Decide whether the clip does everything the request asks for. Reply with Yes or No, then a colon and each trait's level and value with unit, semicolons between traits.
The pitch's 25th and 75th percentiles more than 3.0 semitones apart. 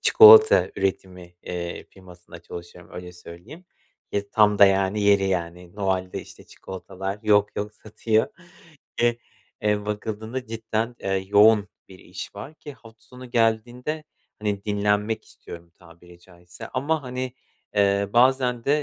Yes: average, 4.0 semitones